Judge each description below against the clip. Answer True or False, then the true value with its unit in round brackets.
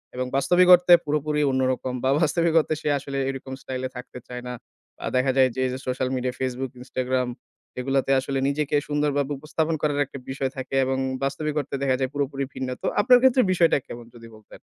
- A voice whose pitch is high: False (135 Hz)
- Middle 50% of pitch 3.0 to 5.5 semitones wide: False (2.6 semitones)